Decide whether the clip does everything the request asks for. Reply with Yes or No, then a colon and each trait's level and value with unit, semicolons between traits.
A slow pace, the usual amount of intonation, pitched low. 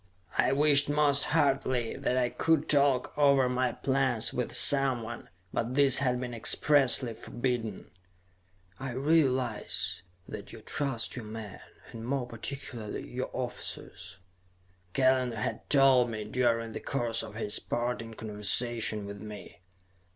Yes: slow, 130 wpm; average, 3.3 semitones; low, 125 Hz